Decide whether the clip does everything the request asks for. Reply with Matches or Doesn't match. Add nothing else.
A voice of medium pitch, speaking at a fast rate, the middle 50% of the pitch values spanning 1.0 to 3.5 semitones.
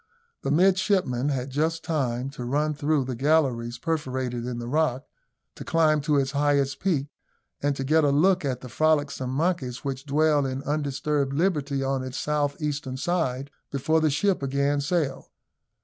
Doesn't match